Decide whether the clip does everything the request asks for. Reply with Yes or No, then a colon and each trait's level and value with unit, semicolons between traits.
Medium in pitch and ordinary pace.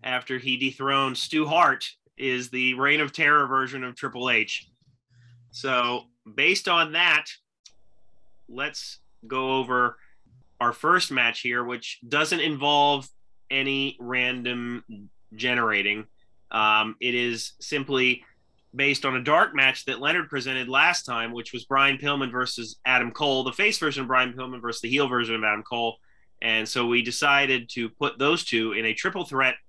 No: low, 130 Hz; average, 155 wpm